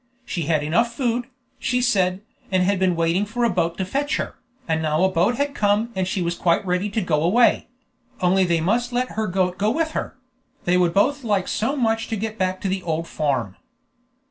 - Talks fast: Yes, fast, 220 wpm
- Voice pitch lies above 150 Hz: Yes, high, 190 Hz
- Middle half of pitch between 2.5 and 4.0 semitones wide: No, average, 4.7 semitones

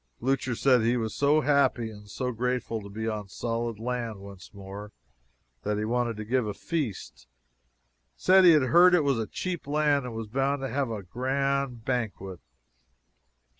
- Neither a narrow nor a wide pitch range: Yes, average, 4.2 semitones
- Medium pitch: No, low, 120 Hz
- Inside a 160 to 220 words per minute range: Yes, average, 180 wpm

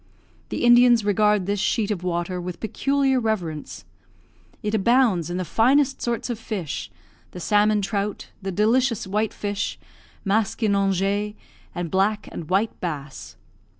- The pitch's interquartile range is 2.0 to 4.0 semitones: Yes, average, 3.3 semitones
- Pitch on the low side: No, high, 205 Hz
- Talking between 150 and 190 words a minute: No, slow, 135 wpm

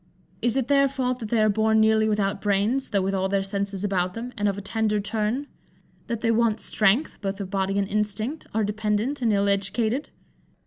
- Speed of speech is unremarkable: No, fast, 210 wpm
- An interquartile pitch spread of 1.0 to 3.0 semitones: Yes, narrow, 2.6 semitones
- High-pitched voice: Yes, high, 215 Hz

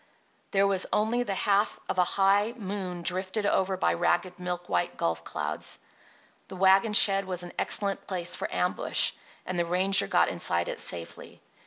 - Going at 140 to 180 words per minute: Yes, average, 170 wpm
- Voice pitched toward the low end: No, high, 190 Hz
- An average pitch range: No, narrow, 2.0 semitones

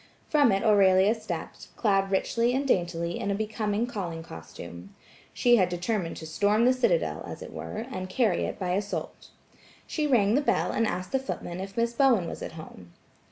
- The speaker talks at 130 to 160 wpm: No, average, 190 wpm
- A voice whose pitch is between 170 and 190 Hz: No, high, 200 Hz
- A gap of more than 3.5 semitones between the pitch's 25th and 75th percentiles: Yes, average, 4.8 semitones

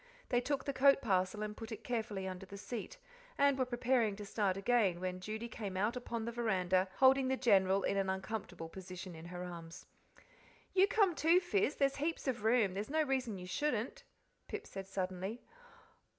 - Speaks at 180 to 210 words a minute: Yes, average, 190 wpm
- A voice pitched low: No, high, 220 Hz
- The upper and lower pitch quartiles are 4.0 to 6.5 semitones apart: Yes, wide, 5.6 semitones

